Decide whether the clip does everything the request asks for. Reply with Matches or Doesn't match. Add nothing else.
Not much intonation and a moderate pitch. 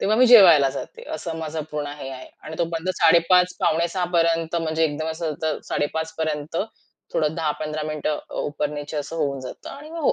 Matches